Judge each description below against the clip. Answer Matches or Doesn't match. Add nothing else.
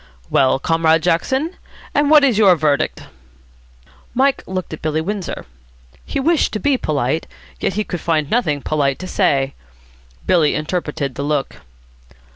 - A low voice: Doesn't match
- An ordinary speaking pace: Matches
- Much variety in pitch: Matches